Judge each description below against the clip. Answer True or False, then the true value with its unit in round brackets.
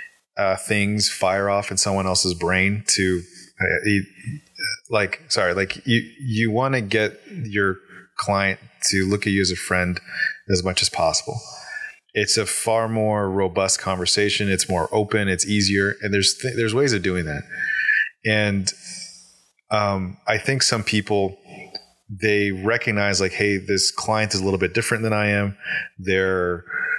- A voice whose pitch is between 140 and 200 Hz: False (100 Hz)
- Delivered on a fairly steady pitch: True (2.2 semitones)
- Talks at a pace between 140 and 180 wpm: True (160 wpm)